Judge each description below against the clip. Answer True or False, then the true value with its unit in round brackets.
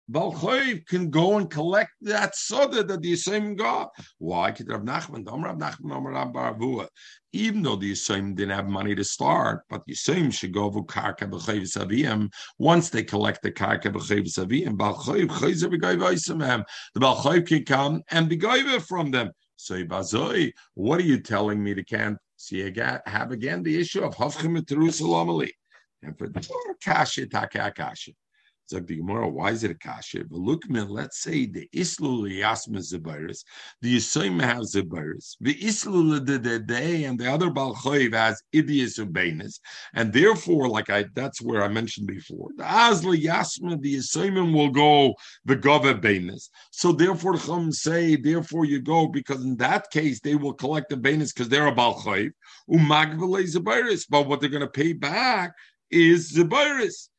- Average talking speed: True (155 wpm)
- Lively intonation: True (7.5 semitones)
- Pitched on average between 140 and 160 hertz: True (145 Hz)